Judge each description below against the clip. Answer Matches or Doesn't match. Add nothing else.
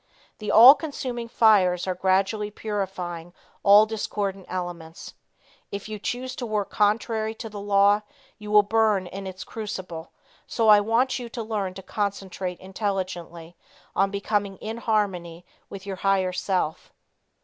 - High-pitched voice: Matches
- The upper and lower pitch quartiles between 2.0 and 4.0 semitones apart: Matches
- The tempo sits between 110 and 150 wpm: Matches